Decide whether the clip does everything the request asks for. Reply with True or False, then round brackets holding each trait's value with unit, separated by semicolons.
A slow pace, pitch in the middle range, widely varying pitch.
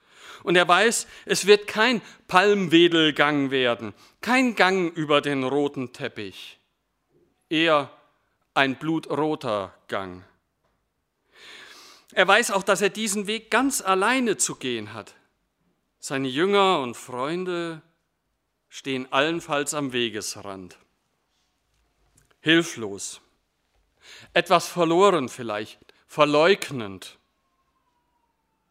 True (90 wpm; 155 Hz; 7.3 semitones)